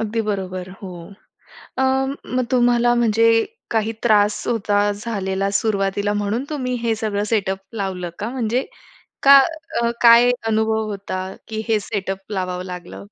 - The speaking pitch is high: Yes, high, 215 Hz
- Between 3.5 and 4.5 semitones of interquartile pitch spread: No, average, 3.0 semitones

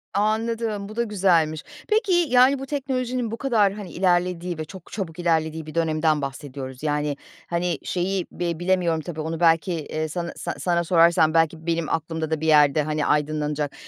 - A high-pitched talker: No, medium, 170 Hz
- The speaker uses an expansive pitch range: No, average, 4.1 semitones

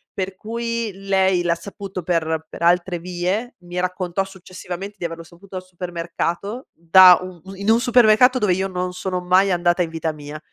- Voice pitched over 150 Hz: Yes, medium, 185 Hz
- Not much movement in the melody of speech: Yes, narrow, 2.2 semitones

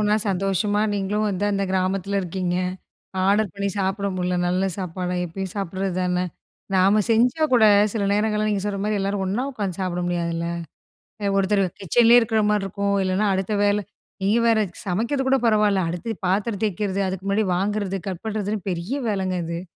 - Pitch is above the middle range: Yes, high, 195 Hz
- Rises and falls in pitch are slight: Yes, narrow, 2.2 semitones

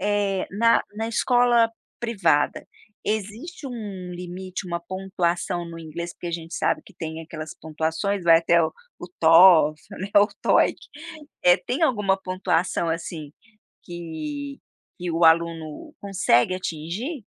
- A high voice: No, medium, 180 Hz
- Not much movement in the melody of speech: No, average, 3.8 semitones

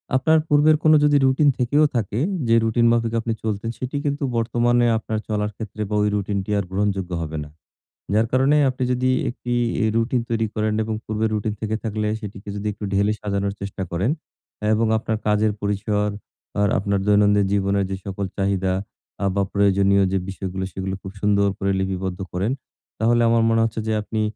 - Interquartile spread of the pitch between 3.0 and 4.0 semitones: No, narrow, 2.6 semitones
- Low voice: Yes, low, 105 Hz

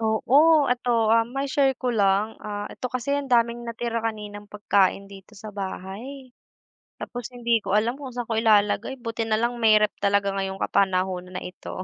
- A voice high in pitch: Yes, high, 220 Hz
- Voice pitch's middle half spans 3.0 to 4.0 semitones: Yes, average, 3.4 semitones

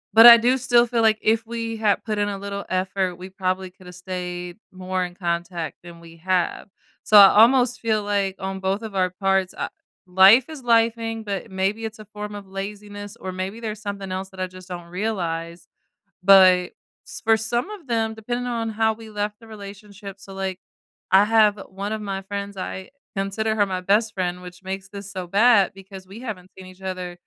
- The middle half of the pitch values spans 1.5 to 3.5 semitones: Yes, average, 2.9 semitones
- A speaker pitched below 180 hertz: No, high, 200 Hz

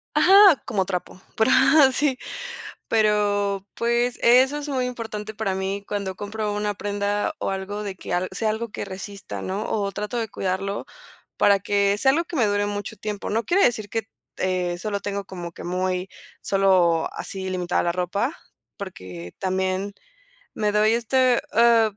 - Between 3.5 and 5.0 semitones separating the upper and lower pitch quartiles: No, average, 2.8 semitones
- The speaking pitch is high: Yes, high, 205 Hz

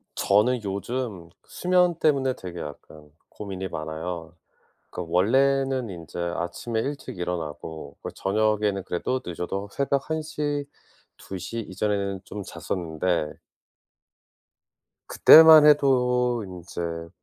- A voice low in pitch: Yes, low, 100 Hz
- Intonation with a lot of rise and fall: Yes, wide, 6.9 semitones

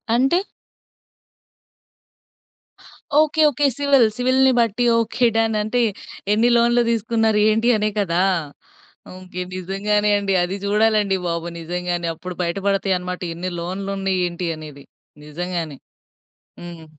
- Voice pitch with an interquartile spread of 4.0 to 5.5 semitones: Yes, average, 4.4 semitones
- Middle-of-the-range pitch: No, high, 195 Hz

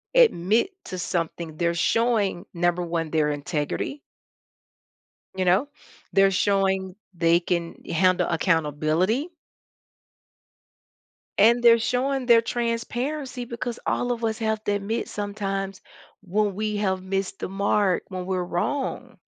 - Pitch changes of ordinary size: Yes, average, 4.7 semitones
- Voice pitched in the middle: No, high, 195 Hz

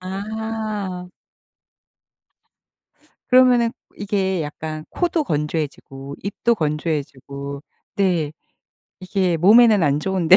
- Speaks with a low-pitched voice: No, medium, 185 Hz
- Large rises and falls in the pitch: Yes, wide, 5.8 semitones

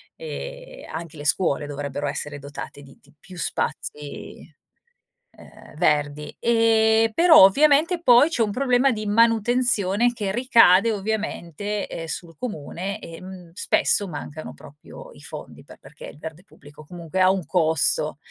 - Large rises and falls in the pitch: Yes, wide, 7.0 semitones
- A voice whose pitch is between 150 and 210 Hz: Yes, high, 190 Hz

